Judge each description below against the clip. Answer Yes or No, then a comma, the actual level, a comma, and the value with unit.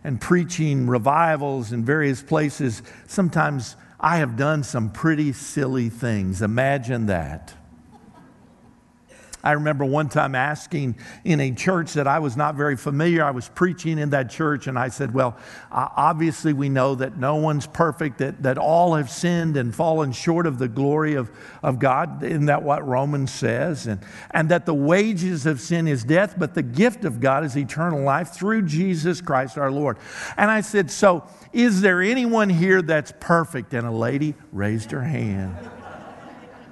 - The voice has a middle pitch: Yes, medium, 145 Hz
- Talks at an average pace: Yes, average, 170 wpm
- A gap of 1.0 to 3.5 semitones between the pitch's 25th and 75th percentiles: No, average, 4.1 semitones